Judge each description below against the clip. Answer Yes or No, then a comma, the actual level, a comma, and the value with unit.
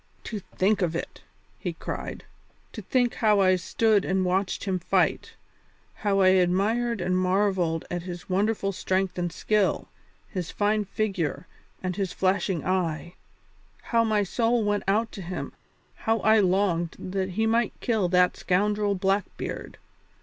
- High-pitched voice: Yes, high, 195 Hz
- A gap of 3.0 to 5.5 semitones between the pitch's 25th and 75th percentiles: No, narrow, 2.6 semitones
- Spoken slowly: No, average, 150 wpm